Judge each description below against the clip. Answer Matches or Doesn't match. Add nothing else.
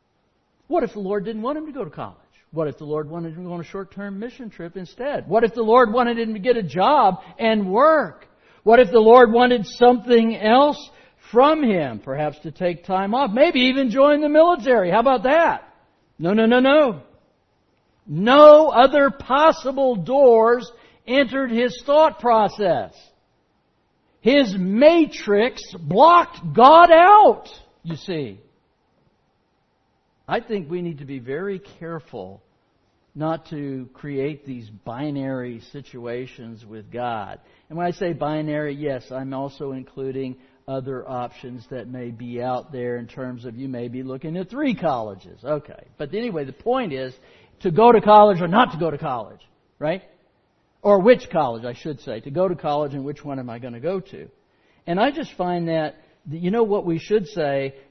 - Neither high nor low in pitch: Matches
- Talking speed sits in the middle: Matches